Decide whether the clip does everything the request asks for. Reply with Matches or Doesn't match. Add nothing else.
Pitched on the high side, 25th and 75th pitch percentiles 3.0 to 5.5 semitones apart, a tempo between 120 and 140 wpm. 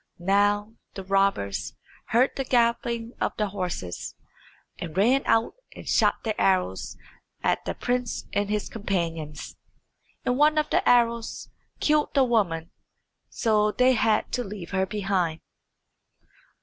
Matches